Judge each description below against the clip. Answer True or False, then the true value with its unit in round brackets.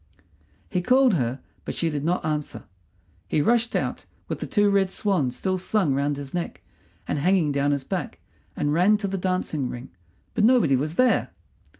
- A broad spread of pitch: True (5.8 semitones)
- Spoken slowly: False (185 wpm)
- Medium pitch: True (170 Hz)